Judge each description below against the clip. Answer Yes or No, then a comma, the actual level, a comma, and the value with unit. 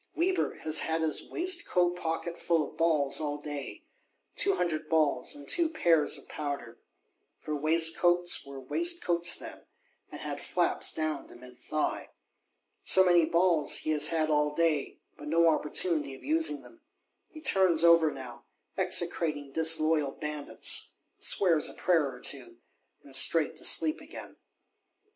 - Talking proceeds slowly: No, average, 150 wpm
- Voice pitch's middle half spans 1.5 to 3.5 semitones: Yes, average, 2.9 semitones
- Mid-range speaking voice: Yes, medium, 160 Hz